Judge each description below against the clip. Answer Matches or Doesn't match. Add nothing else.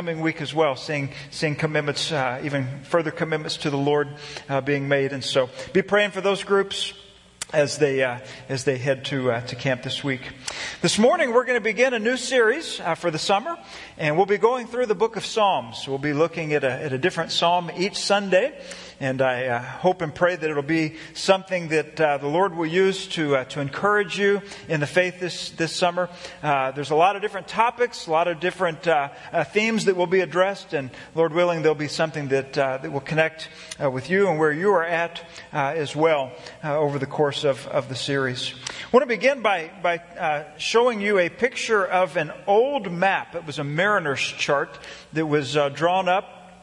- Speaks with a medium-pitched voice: Matches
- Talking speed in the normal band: Doesn't match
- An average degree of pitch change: Matches